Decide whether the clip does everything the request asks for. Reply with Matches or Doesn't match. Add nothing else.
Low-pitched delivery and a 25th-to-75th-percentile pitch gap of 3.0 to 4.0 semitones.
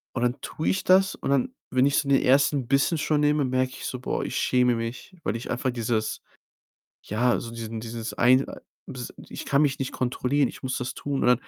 Doesn't match